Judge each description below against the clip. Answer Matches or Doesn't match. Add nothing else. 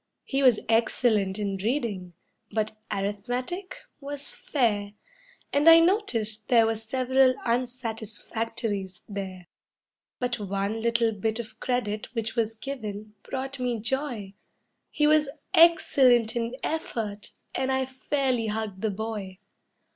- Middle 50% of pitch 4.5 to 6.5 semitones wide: Doesn't match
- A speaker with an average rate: Doesn't match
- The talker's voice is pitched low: Doesn't match